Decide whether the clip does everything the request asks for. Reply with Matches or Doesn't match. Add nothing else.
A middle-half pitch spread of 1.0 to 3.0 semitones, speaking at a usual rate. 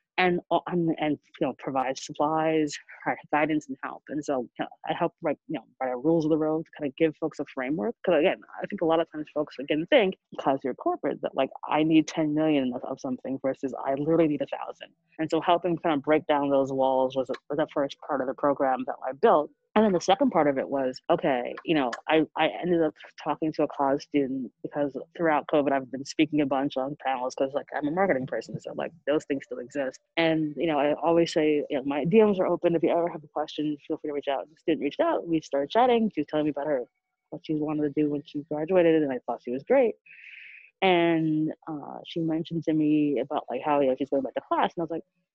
Doesn't match